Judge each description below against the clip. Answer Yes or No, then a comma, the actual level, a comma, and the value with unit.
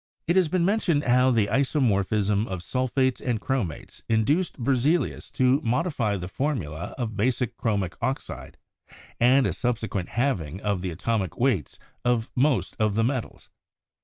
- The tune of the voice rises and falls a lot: No, average, 4.6 semitones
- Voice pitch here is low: Yes, low, 120 Hz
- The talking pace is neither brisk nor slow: Yes, average, 150 wpm